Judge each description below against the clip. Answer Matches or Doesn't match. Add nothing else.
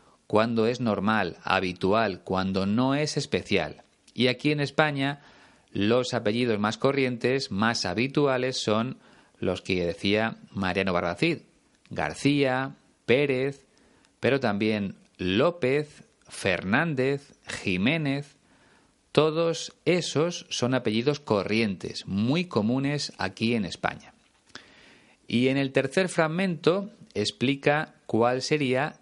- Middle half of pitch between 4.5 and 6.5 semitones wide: Matches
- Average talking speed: Doesn't match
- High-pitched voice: Doesn't match